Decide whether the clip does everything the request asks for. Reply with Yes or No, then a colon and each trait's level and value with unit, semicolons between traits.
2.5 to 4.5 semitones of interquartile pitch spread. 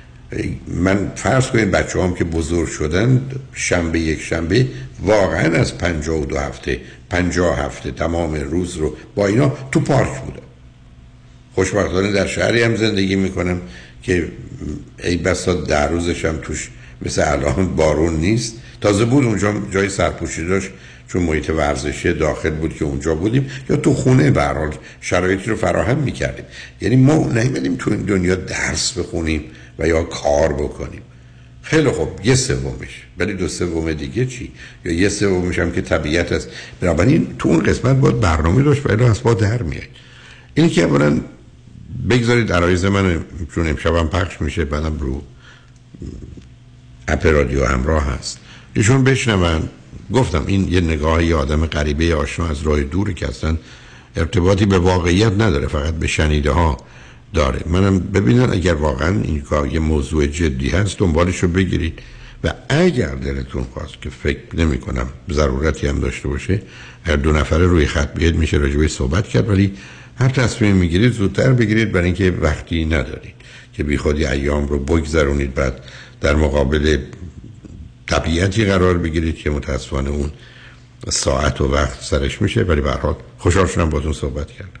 No: average, 5.1 semitones